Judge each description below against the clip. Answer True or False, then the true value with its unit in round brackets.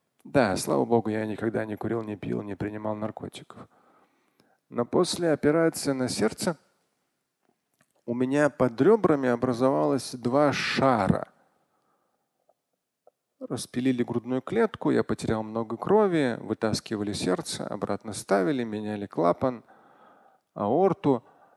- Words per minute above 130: False (105 wpm)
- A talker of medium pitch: False (120 Hz)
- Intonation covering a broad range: False (4.7 semitones)